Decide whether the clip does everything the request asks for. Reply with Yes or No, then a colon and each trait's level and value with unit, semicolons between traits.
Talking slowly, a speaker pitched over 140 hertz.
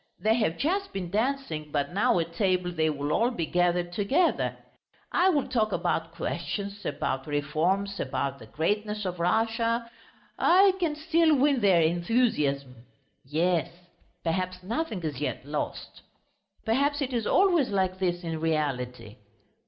No: average, 145 wpm; medium, 185 Hz